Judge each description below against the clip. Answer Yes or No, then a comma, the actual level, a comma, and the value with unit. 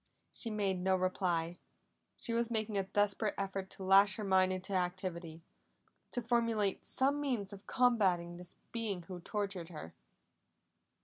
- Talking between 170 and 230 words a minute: No, average, 145 wpm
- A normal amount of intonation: Yes, average, 3.0 semitones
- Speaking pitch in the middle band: No, high, 195 Hz